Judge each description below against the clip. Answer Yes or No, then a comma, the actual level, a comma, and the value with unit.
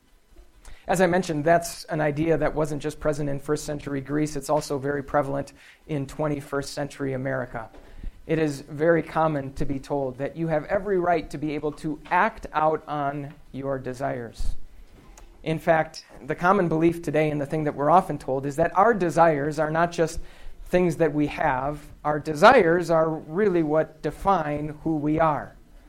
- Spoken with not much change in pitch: Yes, narrow, 2.3 semitones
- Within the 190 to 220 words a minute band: No, average, 175 wpm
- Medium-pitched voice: Yes, medium, 150 Hz